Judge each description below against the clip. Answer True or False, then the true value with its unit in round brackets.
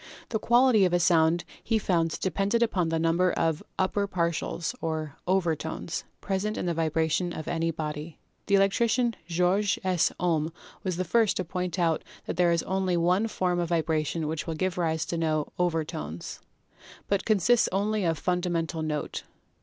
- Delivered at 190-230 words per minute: False (175 wpm)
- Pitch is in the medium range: True (175 Hz)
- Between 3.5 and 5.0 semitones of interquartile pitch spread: False (2.9 semitones)